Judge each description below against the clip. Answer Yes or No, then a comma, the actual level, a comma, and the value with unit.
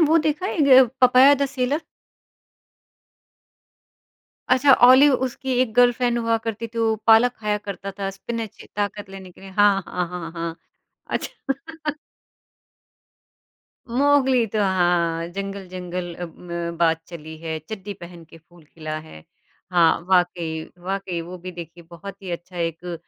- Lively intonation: Yes, wide, 5.7 semitones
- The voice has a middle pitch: No, high, 195 Hz